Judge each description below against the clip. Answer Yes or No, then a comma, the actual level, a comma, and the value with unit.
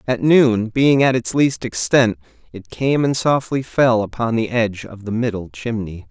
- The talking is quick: No, average, 185 wpm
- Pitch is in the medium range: No, low, 115 Hz